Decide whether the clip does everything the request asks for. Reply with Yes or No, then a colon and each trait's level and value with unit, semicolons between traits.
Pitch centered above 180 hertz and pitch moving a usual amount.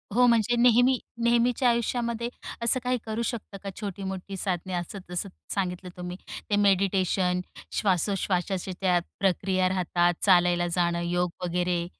Yes: high, 190 Hz; average, 3.8 semitones